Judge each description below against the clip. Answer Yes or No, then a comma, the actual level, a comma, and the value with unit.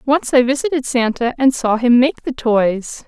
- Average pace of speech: Yes, average, 195 wpm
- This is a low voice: No, very high, 250 Hz